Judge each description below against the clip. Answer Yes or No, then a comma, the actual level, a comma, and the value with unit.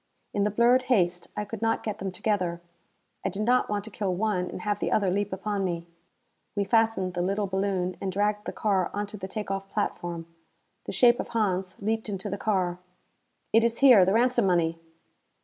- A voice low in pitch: No, high, 200 Hz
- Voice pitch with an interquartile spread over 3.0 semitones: No, average, 2.7 semitones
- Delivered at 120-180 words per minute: No, average, 200 wpm